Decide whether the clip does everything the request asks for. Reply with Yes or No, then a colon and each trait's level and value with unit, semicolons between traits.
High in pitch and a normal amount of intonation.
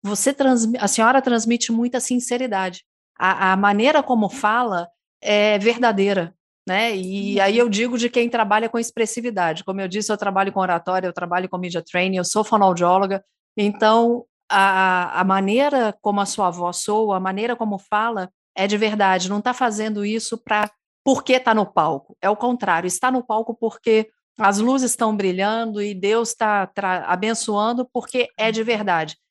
Yes: high, 210 Hz; average, 3.4 semitones